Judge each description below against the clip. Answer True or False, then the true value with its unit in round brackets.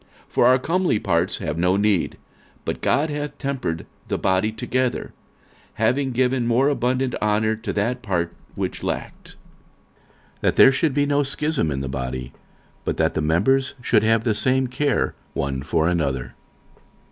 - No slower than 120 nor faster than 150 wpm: False (165 wpm)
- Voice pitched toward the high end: False (115 Hz)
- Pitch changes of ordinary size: False (7.4 semitones)